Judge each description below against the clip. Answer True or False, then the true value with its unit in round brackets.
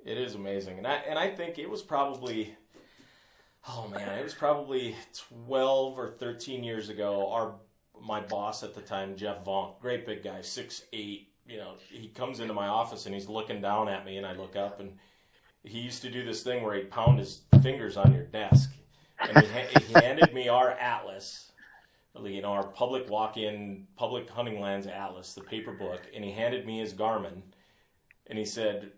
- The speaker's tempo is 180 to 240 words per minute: True (200 wpm)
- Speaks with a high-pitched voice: False (110 Hz)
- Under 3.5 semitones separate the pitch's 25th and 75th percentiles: False (4.2 semitones)